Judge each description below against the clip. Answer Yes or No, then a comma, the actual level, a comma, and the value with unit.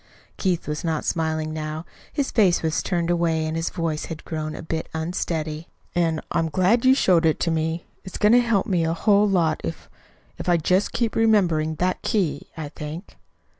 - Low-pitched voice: No, medium, 165 Hz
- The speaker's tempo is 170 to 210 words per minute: Yes, average, 195 wpm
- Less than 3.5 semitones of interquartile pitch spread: Yes, average, 2.9 semitones